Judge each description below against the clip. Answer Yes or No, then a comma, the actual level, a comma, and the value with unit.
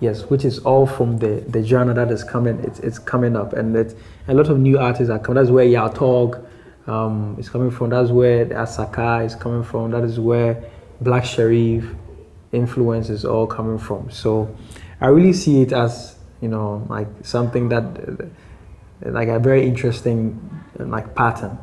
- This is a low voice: Yes, low, 120 Hz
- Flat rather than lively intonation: Yes, narrow, 1.8 semitones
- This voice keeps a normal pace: Yes, average, 180 wpm